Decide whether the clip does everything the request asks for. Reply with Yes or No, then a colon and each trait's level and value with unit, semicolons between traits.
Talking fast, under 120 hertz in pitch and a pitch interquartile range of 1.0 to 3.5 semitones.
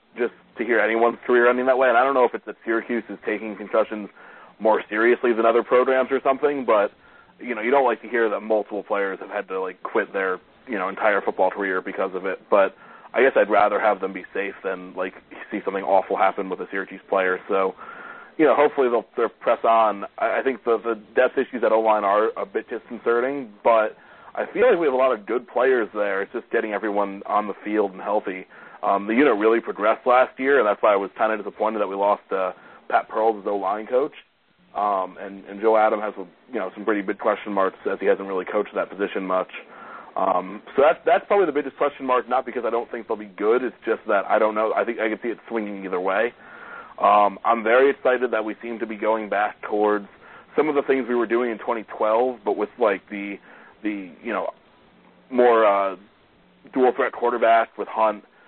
Yes: fast, 230 wpm; low, 110 Hz; average, 2.9 semitones